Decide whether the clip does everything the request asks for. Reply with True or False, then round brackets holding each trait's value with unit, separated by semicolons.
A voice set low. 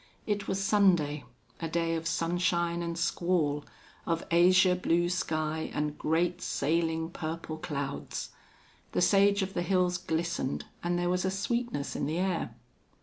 False (170 Hz)